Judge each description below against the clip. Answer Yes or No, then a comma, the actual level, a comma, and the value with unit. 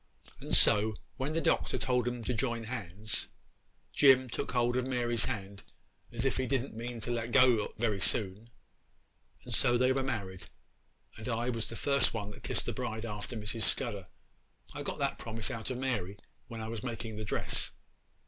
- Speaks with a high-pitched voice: No, low, 115 Hz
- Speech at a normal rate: Yes, average, 185 wpm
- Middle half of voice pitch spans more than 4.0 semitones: No, average, 2.7 semitones